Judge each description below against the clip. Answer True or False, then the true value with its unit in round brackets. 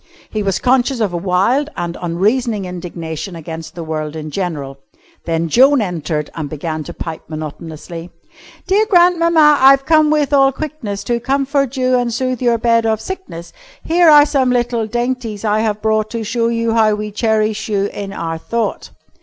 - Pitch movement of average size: False (7.0 semitones)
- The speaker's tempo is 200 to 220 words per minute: False (175 wpm)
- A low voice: False (220 Hz)